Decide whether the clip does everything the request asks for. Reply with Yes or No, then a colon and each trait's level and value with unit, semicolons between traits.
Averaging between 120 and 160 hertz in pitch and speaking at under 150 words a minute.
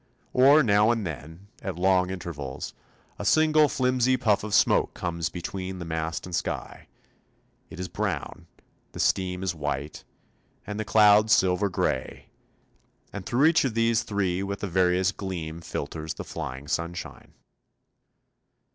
No: very low, 95 Hz; average, 140 wpm